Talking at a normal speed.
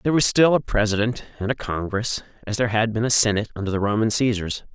No: fast, 225 wpm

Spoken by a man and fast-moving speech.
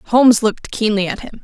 No: female; fast, 210 wpm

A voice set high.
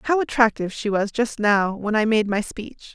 Yes: high, 220 Hz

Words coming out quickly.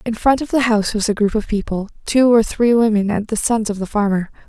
Yes: fast, 270 wpm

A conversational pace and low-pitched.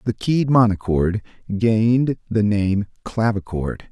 No: slow, 105 wpm; low, 105 Hz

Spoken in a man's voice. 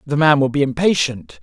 Yes: male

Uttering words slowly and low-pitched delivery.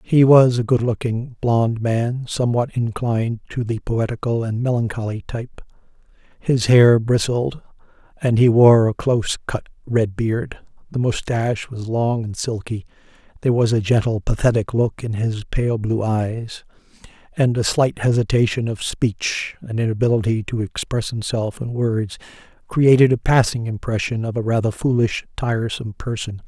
No: average, 150 wpm; low, 115 Hz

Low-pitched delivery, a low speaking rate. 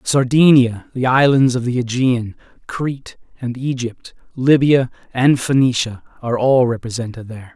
Yes: low, 125 Hz; slow, 125 wpm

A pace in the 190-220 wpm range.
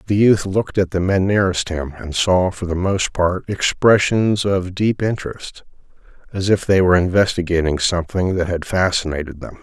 No: average, 175 wpm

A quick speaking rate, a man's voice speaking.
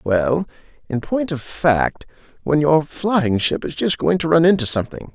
No: average, 185 wpm; male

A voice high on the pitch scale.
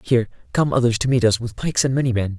No: low, 120 Hz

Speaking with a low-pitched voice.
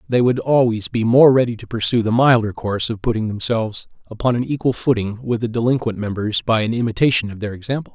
Yes: low, 115 Hz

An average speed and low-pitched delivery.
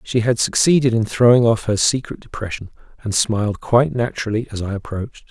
Yes: average, 180 wpm; low, 115 Hz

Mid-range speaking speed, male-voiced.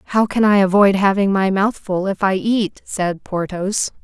No: average, 195 wpm; female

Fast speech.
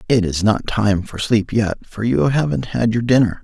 Yes: fast, 225 wpm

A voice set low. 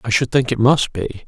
Yes: low, 120 Hz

